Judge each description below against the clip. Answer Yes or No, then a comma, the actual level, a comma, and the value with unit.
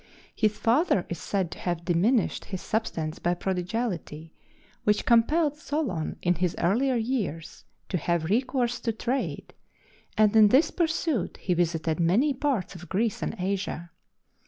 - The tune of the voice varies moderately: No, wide, 6.0 semitones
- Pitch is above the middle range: Yes, high, 205 Hz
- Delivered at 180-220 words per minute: No, average, 145 wpm